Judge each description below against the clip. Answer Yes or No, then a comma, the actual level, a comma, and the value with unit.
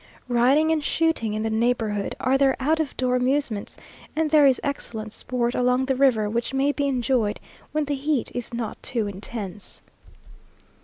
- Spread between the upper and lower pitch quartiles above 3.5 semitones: Yes, average, 3.9 semitones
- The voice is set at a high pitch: Yes, very high, 250 Hz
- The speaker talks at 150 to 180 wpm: Yes, average, 170 wpm